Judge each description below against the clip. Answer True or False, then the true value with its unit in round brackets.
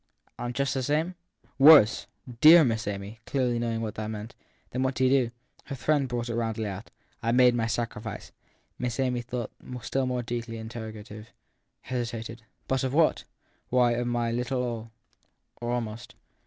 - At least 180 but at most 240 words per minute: True (185 wpm)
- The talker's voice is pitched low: True (120 Hz)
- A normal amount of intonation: False (2.2 semitones)